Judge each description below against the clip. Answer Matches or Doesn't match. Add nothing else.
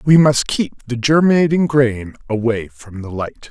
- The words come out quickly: Doesn't match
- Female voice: Doesn't match